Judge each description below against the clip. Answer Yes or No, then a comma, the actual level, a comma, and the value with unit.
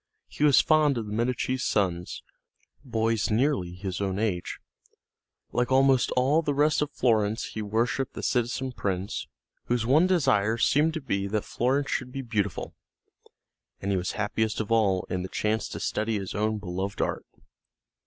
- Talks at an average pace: Yes, average, 165 wpm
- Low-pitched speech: Yes, low, 110 Hz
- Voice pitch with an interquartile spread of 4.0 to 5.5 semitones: Yes, average, 4.5 semitones